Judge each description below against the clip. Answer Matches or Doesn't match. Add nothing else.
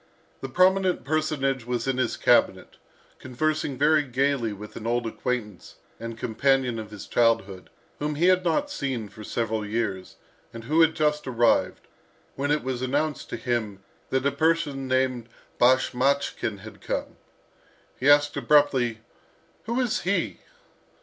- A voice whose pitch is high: Doesn't match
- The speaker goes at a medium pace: Matches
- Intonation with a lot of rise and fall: Doesn't match